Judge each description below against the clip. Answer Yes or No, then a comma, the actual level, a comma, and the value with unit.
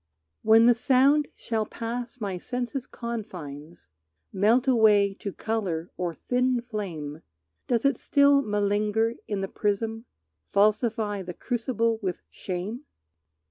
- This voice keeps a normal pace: No, slow, 120 wpm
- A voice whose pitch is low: No, high, 220 Hz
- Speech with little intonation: No, average, 3.4 semitones